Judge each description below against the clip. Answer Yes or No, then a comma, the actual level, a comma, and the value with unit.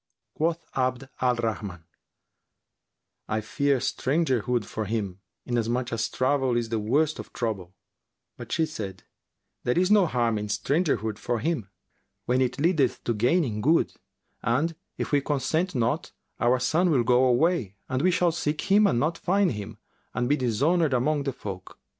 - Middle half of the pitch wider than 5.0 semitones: Yes, wide, 5.6 semitones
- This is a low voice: Yes, low, 130 Hz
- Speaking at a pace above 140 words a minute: Yes, average, 160 wpm